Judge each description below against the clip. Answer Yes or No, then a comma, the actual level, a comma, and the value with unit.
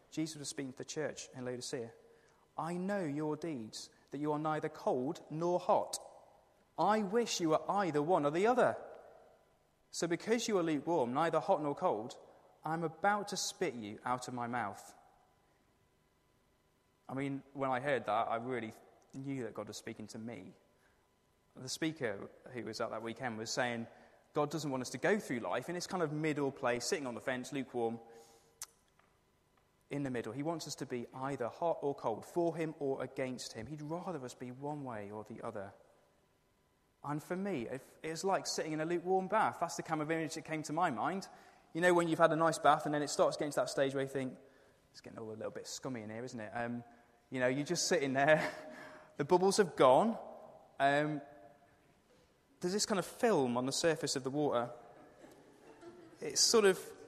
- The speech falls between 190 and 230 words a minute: Yes, average, 200 wpm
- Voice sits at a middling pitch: Yes, medium, 145 Hz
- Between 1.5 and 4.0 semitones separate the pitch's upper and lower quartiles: No, average, 5.1 semitones